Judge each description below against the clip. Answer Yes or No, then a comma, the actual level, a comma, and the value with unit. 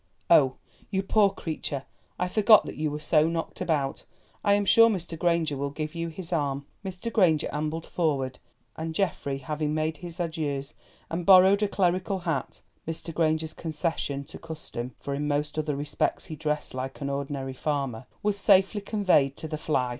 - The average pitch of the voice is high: No, medium, 155 Hz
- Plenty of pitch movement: No, average, 3.8 semitones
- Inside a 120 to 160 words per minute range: No, average, 175 wpm